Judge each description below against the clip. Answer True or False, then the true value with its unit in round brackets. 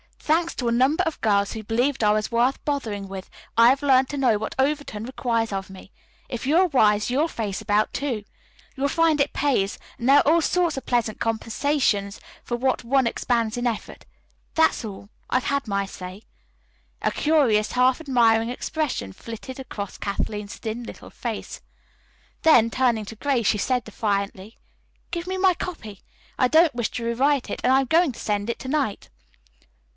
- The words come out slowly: False (185 wpm)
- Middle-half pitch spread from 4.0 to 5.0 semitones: True (4.7 semitones)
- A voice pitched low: False (240 Hz)